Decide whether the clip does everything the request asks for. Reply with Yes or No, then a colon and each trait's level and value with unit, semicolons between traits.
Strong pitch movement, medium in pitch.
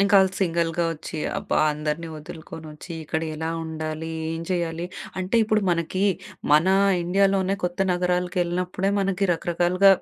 No: narrow, 2.4 semitones; medium, 175 Hz